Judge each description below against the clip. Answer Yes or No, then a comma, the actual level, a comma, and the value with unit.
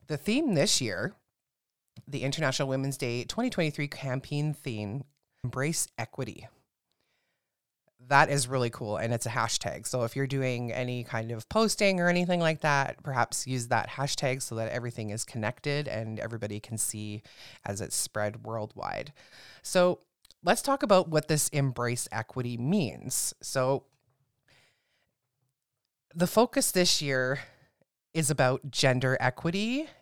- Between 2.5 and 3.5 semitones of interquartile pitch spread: No, average, 3.9 semitones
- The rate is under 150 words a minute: Yes, slow, 135 wpm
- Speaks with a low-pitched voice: Yes, low, 130 Hz